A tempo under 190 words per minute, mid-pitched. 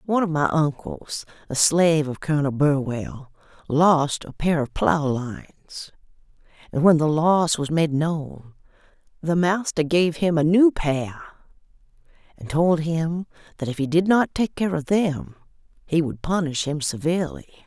Yes: average, 155 wpm; medium, 155 Hz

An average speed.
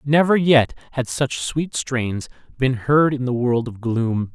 Yes: average, 180 wpm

